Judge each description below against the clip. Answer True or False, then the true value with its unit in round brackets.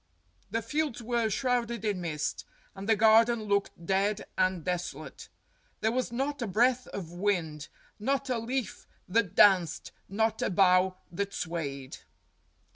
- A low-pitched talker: False (205 Hz)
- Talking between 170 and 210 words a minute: False (145 wpm)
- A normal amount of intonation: True (4.5 semitones)